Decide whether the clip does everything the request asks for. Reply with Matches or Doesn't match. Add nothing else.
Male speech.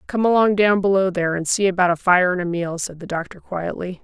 Doesn't match